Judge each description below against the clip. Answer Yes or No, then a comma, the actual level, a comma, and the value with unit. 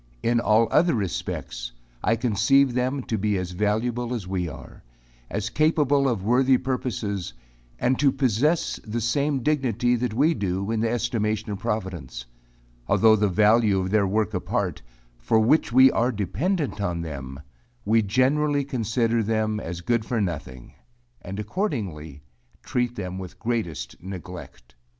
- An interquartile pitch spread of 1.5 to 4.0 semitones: No, average, 4.6 semitones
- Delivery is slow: No, average, 150 wpm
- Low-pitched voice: Yes, low, 110 Hz